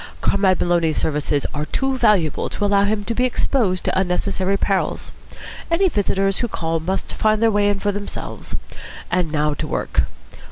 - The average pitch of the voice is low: No, high, 195 Hz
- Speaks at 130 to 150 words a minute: No, average, 170 wpm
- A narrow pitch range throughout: No, average, 3.3 semitones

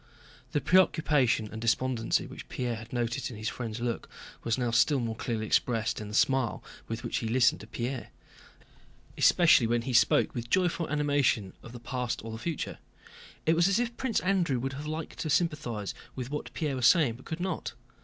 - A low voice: Yes, low, 125 Hz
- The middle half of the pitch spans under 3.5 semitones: No, average, 4.8 semitones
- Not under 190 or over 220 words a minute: Yes, average, 195 wpm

